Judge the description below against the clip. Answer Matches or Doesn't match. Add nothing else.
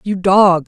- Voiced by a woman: Matches